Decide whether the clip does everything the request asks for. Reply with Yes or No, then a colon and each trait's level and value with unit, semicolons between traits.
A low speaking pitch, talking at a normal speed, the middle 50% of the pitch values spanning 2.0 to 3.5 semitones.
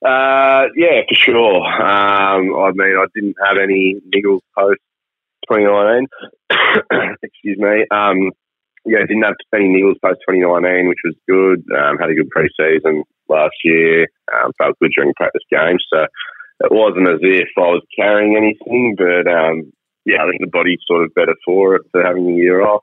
Yes: very low, 95 Hz; average, 180 wpm; narrow, 2.4 semitones